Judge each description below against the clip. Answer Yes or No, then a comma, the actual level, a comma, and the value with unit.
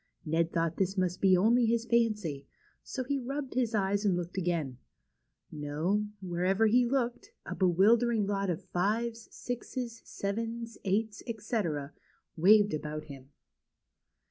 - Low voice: No, high, 200 Hz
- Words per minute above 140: No, slow, 135 wpm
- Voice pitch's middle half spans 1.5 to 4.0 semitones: No, average, 5.0 semitones